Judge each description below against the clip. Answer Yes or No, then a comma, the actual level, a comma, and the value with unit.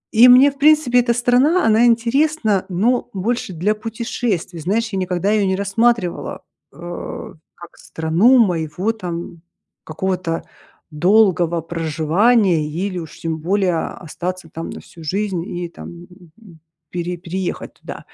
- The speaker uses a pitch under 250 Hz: Yes, high, 190 Hz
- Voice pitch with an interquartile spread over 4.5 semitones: Yes, average, 5.1 semitones